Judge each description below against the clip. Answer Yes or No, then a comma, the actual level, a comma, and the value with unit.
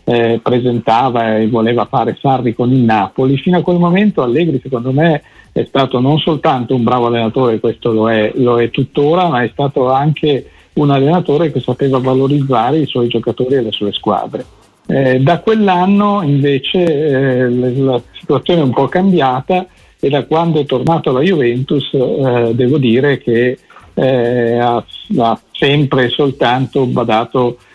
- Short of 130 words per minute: No, average, 160 wpm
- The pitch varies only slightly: No, average, 3.4 semitones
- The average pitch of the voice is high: No, low, 130 Hz